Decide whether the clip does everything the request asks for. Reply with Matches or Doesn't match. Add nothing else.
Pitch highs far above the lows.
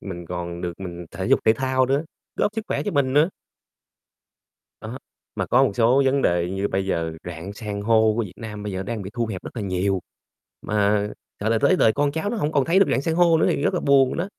Matches